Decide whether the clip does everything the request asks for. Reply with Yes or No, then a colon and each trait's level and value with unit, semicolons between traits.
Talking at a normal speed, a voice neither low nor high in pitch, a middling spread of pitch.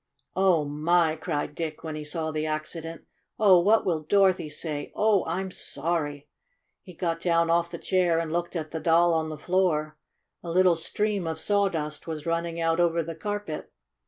No: average, 180 wpm; medium, 165 Hz; narrow, 2.3 semitones